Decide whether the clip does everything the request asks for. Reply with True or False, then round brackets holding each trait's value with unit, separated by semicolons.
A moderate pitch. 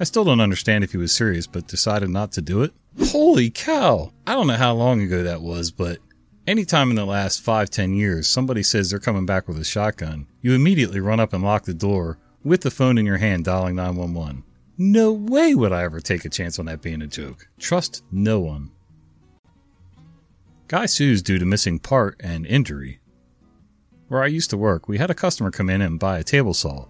False (100 Hz)